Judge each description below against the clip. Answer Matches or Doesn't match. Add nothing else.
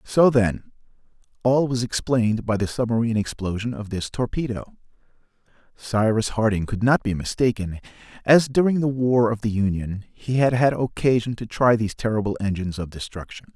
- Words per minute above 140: Matches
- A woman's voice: Doesn't match